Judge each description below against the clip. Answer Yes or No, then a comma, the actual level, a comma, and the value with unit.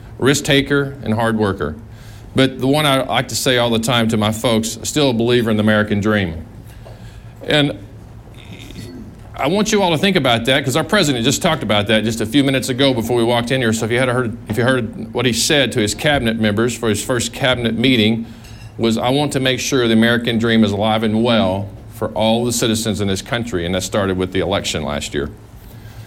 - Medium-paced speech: No, fast, 225 wpm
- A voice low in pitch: Yes, low, 115 Hz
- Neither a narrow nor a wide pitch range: Yes, average, 3.1 semitones